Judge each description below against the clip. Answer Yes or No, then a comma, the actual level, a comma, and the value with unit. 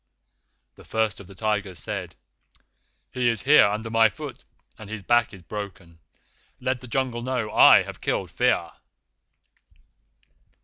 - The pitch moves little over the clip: No, average, 3.4 semitones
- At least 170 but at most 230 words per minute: No, average, 140 wpm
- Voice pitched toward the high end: No, low, 110 Hz